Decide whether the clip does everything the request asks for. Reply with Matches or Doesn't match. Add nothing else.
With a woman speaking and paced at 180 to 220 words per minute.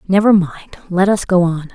Matches